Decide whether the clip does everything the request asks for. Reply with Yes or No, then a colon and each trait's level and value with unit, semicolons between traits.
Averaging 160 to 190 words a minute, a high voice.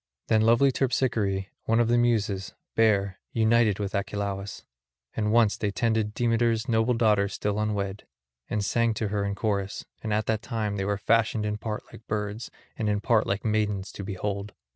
No: average, 180 wpm; low, 105 Hz